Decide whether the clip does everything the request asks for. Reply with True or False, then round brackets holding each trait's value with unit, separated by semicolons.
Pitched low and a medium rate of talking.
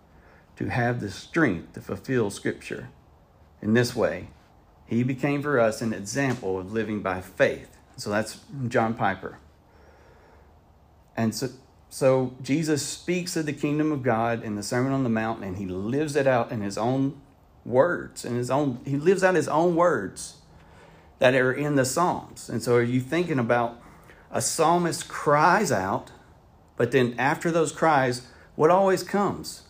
True (130 Hz; 165 wpm)